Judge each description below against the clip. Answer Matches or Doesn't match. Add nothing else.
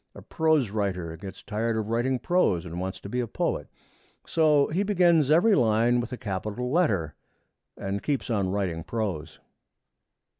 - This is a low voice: Matches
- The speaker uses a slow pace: Doesn't match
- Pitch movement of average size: Doesn't match